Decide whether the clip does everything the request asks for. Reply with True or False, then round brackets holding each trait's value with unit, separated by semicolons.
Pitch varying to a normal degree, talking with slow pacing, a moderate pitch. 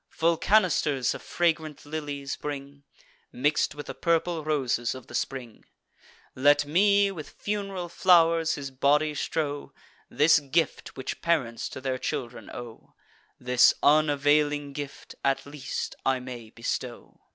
True (3.4 semitones; 130 wpm; 145 Hz)